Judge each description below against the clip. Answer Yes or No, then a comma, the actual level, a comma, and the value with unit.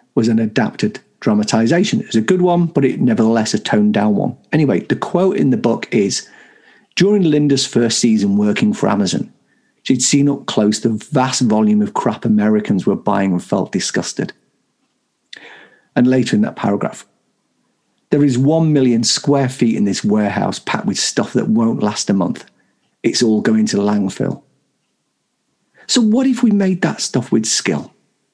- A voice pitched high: No, low, 130 Hz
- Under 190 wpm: Yes, average, 170 wpm